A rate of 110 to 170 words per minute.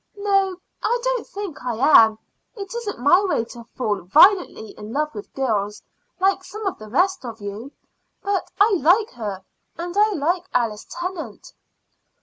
Yes: average, 160 wpm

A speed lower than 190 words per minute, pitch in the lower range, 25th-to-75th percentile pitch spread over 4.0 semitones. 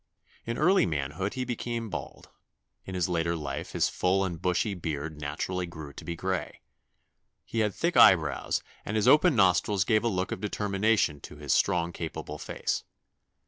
Yes: average, 170 wpm; very low, 90 Hz; average, 4.8 semitones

